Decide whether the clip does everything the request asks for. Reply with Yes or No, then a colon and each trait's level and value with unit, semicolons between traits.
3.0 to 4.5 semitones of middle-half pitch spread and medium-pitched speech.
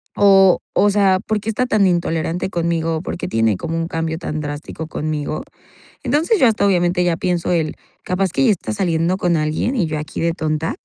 Yes: average, 3.3 semitones; medium, 170 Hz